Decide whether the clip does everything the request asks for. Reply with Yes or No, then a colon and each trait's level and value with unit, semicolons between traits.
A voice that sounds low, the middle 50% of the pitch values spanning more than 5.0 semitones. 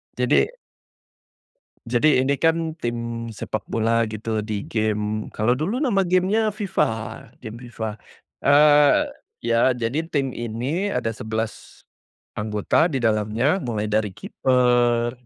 Yes: low, 120 Hz; wide, 5.4 semitones